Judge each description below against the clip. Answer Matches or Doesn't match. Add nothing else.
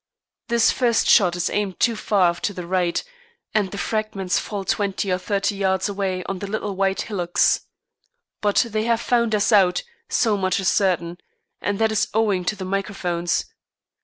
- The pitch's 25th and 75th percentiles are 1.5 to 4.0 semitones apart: Matches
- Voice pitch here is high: Matches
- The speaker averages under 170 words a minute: Doesn't match